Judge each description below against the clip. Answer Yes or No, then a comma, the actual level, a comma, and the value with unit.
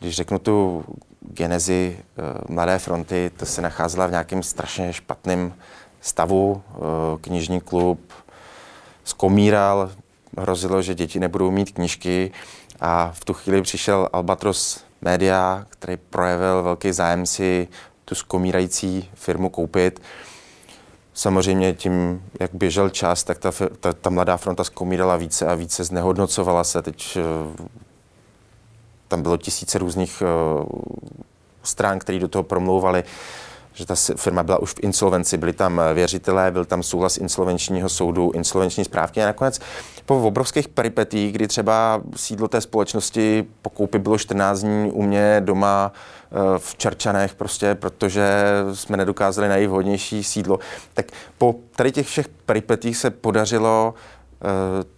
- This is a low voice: Yes, very low, 95 Hz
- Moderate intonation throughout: No, narrow, 2.2 semitones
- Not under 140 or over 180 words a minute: No, average, 130 wpm